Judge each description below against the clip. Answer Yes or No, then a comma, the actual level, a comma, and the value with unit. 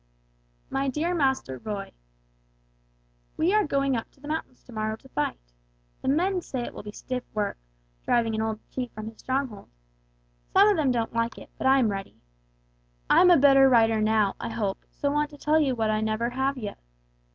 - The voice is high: Yes, very high, 250 Hz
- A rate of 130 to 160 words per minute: No, average, 200 wpm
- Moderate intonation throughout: Yes, average, 4.3 semitones